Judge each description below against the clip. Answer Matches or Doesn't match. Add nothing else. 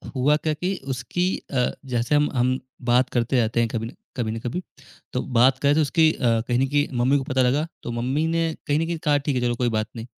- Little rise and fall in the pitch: Doesn't match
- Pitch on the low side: Matches